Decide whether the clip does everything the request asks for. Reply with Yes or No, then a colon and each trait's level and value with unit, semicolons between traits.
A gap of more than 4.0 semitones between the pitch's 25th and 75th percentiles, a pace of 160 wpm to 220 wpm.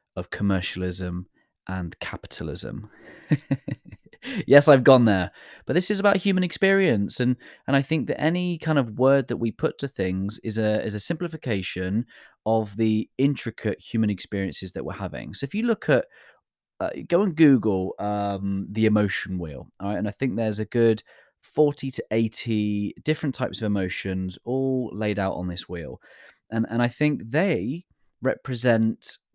Yes: wide, 5.6 semitones; average, 165 wpm